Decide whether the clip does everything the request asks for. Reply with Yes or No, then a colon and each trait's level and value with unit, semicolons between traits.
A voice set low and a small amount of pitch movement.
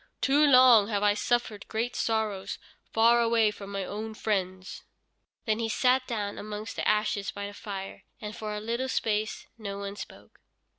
No: high, 215 Hz; narrow, 2.2 semitones